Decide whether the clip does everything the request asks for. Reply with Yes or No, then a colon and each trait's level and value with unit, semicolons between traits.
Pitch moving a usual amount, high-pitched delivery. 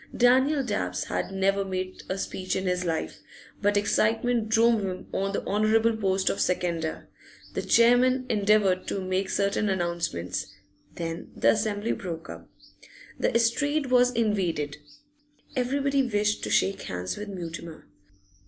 Yes: average, 4.1 semitones; high, 200 Hz